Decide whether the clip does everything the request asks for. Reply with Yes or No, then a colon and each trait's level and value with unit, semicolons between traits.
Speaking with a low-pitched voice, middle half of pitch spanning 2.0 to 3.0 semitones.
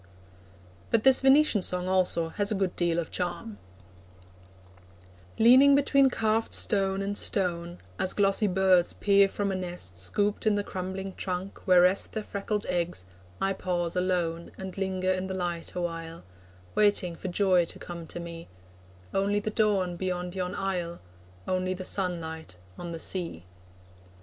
No: medium, 185 Hz; narrow, 2.4 semitones